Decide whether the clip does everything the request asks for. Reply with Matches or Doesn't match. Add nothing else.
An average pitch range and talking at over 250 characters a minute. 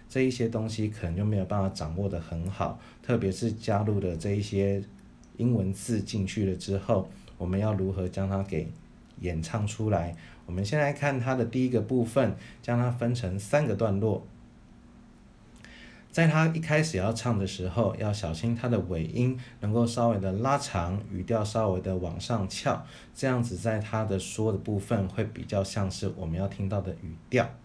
Matches